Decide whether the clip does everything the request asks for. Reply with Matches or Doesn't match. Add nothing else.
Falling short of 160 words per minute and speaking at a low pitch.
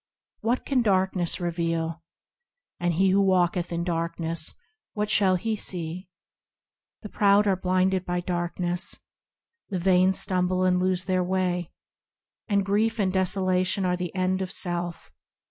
Doesn't match